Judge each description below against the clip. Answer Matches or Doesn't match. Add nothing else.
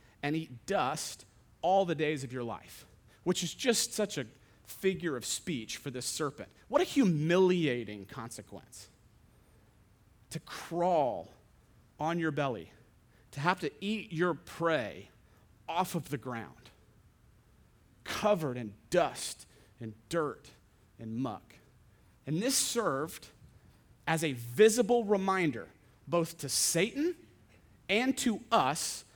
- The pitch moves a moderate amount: Doesn't match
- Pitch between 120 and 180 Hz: Matches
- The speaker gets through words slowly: Matches